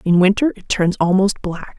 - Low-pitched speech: No, high, 190 Hz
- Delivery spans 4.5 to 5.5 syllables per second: Yes, 4.9 syllables/s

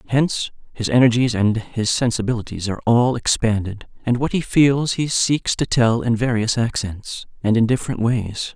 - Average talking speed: Yes, average, 170 wpm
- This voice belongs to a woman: No, male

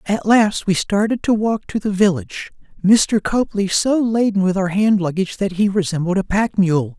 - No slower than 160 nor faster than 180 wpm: No, average, 195 wpm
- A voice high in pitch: Yes, high, 200 Hz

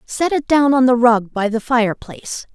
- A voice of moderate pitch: No, high, 245 Hz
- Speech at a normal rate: No, fast, 235 wpm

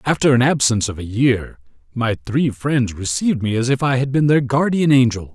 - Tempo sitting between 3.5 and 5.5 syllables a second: Yes, 5.4 syllables/s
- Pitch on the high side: No, low, 125 Hz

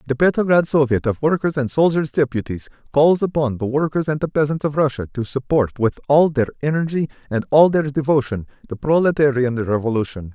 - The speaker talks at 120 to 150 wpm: No, average, 175 wpm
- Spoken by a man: Yes, male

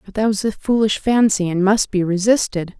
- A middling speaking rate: No, fast, 215 wpm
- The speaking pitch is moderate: No, high, 205 Hz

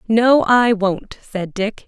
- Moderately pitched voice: No, high, 215 Hz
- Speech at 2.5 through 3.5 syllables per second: Yes, 3.2 syllables/s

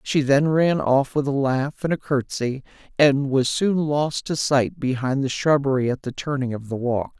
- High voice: No, medium, 140 Hz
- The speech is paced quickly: Yes, fast, 210 wpm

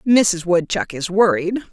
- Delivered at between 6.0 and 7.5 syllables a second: No, 4.1 syllables/s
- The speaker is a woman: Yes, female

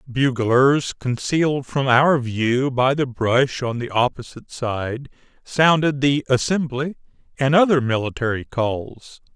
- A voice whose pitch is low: Yes, low, 130 Hz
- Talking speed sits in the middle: No, slow, 120 wpm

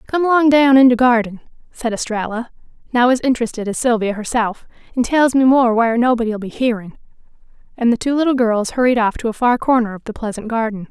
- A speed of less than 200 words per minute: No, fast, 205 wpm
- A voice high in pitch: Yes, high, 240 Hz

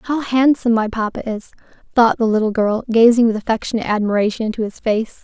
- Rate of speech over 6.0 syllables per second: Yes, 6.2 syllables/s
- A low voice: No, high, 225 Hz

